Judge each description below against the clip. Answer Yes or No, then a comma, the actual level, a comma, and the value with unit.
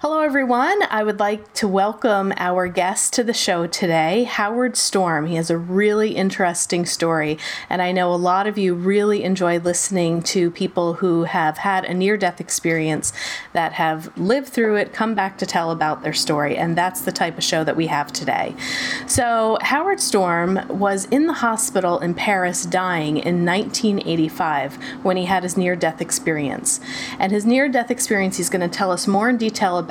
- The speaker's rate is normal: Yes, average, 185 wpm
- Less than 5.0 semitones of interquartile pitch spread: Yes, average, 3.9 semitones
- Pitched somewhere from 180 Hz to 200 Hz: Yes, high, 190 Hz